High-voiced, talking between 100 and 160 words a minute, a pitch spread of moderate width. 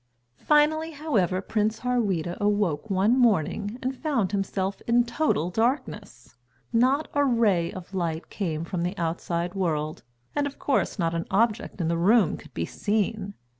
No: high, 205 Hz; average, 155 wpm; wide, 5.7 semitones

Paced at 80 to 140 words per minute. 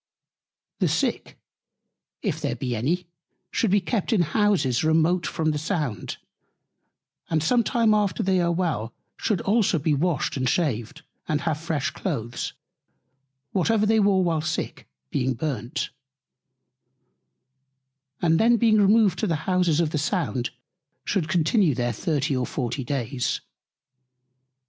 Yes: slow, 135 wpm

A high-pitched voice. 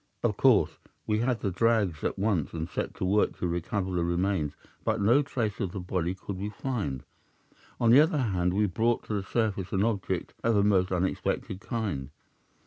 No: low, 100 Hz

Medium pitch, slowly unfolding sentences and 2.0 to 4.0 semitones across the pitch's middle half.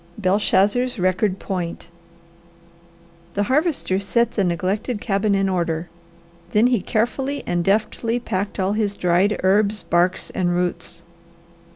No: high, 200 Hz; slow, 125 wpm; average, 3.1 semitones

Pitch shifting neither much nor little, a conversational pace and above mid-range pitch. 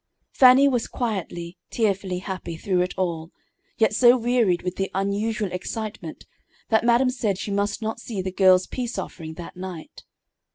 Yes: average, 3.9 semitones; average, 160 wpm; high, 200 Hz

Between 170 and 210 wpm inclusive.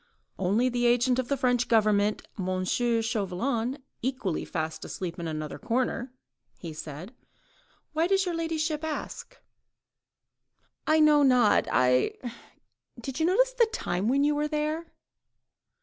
No: slow, 135 wpm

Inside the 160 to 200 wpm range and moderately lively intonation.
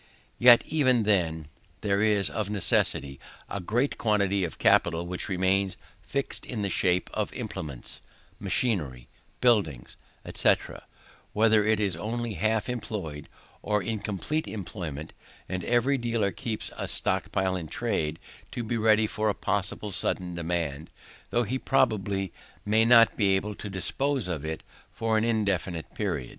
No: average, 145 wpm; average, 4.0 semitones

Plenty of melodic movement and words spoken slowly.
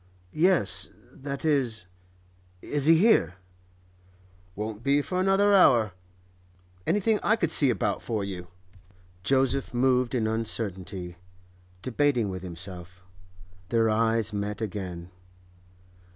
Yes: wide, 7.0 semitones; slow, 105 wpm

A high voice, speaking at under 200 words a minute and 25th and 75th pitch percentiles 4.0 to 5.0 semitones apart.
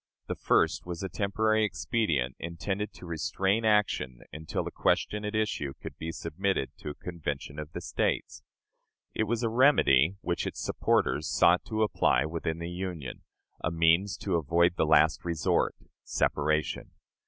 No: very low, 85 Hz; average, 155 wpm; average, 4.7 semitones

